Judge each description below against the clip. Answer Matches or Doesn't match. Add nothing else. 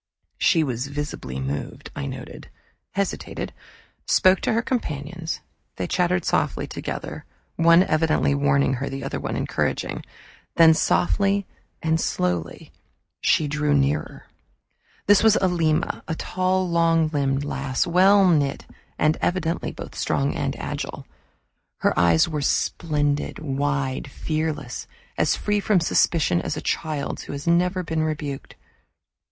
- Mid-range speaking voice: Matches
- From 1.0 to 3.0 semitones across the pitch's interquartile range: Doesn't match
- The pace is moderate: Doesn't match